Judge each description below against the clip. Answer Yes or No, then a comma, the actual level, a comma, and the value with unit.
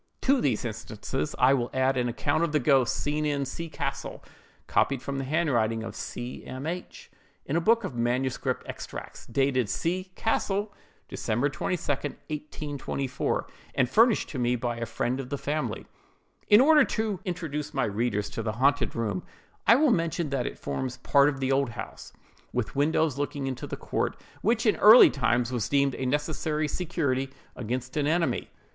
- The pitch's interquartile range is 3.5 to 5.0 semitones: Yes, average, 4.4 semitones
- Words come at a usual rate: Yes, average, 175 wpm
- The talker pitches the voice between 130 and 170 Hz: Yes, medium, 140 Hz